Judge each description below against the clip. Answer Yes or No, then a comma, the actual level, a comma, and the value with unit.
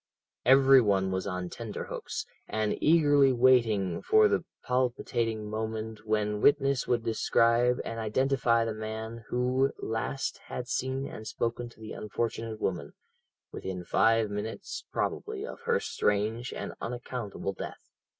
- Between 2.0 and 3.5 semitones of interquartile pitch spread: Yes, average, 3.2 semitones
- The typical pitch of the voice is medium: No, low, 115 Hz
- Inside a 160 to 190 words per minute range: No, slow, 135 wpm